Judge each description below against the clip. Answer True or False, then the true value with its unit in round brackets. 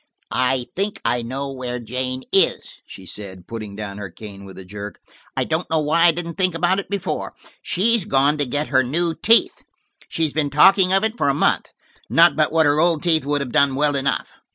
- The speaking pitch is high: False (145 Hz)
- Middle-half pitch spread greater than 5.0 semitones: True (5.5 semitones)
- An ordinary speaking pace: False (215 wpm)